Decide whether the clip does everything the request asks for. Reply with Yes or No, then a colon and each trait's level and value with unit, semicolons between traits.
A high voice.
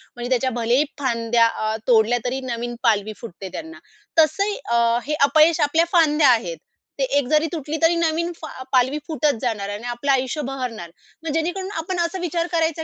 Yes: very high, 270 Hz